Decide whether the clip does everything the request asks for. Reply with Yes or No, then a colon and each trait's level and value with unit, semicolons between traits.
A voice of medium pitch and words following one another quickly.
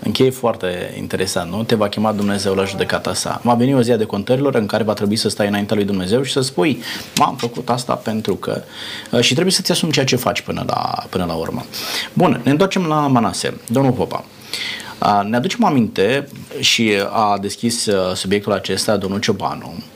No: low, 110 Hz; fast, 190 wpm